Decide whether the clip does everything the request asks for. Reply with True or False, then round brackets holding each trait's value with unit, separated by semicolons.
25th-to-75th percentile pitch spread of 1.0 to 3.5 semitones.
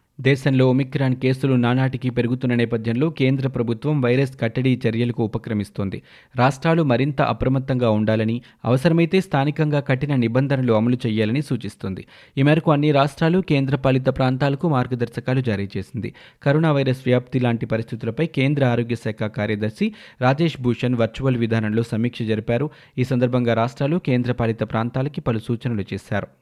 True (3.1 semitones)